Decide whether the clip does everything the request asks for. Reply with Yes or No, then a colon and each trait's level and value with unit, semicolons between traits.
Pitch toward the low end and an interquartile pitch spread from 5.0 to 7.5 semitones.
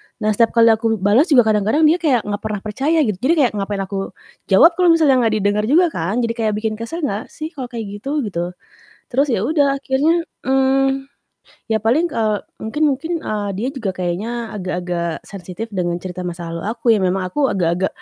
No: high, 225 Hz; wide, 5.6 semitones